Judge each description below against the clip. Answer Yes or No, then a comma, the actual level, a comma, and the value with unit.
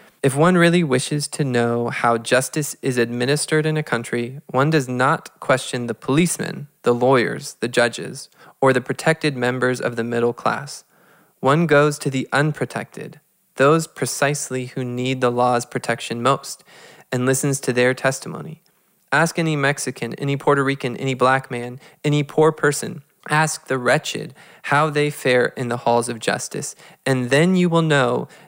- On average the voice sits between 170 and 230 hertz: No, low, 135 Hz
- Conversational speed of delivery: Yes, average, 160 wpm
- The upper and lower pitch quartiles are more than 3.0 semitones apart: Yes, average, 3.5 semitones